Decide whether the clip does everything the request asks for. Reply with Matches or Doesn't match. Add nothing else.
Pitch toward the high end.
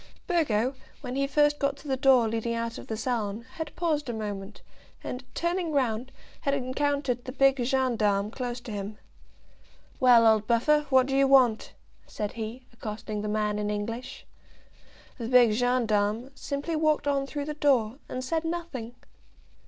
Matches